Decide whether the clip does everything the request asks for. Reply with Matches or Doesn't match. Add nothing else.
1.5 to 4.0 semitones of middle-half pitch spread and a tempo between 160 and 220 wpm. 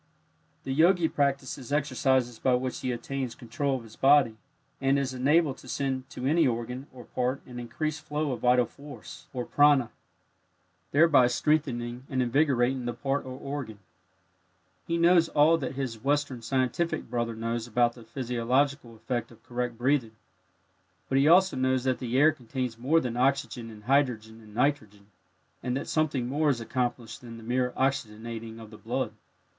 Matches